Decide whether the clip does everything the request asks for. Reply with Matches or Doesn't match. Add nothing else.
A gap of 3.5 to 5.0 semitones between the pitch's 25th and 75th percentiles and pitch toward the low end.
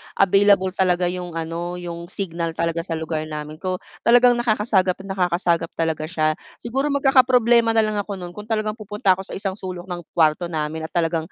Doesn't match